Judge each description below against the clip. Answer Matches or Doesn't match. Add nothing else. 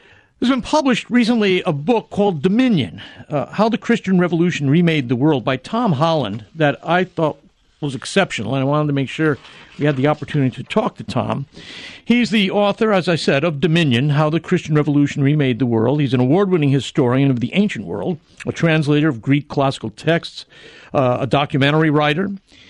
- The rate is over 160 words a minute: Matches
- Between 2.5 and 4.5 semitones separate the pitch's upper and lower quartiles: Doesn't match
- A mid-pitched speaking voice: Matches